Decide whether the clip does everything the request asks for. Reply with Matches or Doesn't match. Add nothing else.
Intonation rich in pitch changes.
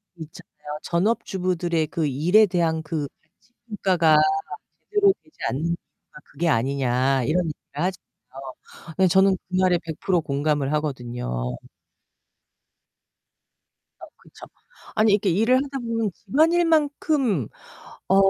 Matches